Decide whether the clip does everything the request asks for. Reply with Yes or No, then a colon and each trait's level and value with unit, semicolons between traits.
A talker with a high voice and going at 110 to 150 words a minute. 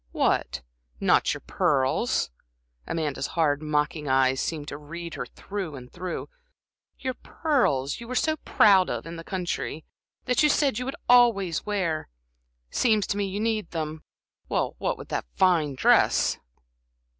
No: medium, 170 Hz; average, 145 wpm